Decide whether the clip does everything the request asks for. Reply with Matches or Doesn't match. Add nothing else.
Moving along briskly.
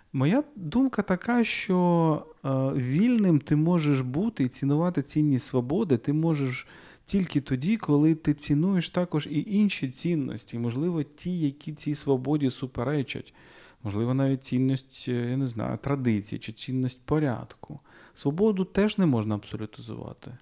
Doesn't match